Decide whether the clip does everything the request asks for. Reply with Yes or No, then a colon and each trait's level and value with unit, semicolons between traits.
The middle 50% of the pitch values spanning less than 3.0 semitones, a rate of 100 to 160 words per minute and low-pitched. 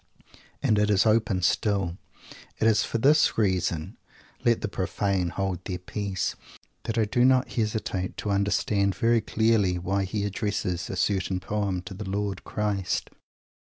Yes: narrow, 2.5 semitones; average, 155 wpm; low, 100 Hz